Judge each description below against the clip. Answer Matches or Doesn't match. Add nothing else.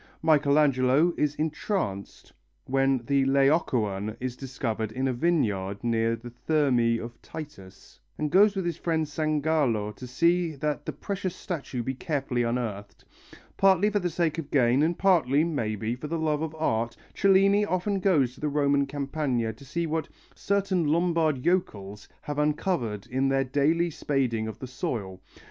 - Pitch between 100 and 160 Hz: Matches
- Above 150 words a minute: Matches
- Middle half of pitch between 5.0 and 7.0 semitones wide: Matches